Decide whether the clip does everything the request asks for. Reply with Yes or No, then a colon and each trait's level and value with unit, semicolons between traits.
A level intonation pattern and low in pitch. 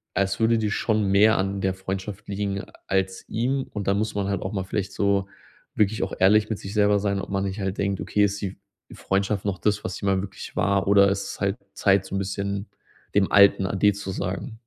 Yes: narrow, 1.1 semitones; low, 100 Hz